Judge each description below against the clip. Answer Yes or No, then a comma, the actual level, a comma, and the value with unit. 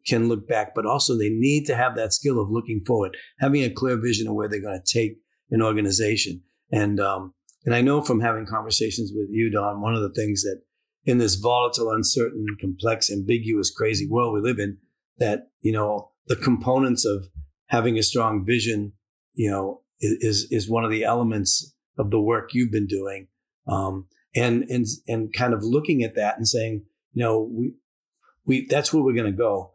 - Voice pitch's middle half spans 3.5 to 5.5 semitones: No, narrow, 2.6 semitones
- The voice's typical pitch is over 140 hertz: No, low, 110 Hz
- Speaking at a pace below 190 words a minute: No, average, 200 wpm